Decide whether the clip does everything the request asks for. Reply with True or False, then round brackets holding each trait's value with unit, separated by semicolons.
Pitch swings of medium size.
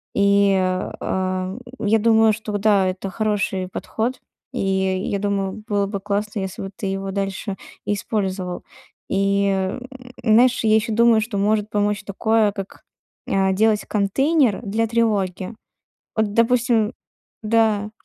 False (2.2 semitones)